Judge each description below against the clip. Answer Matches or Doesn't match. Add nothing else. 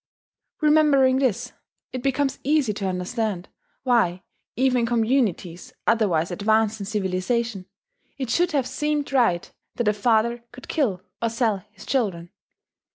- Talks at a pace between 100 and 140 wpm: Matches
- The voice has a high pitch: Matches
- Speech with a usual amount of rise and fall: Matches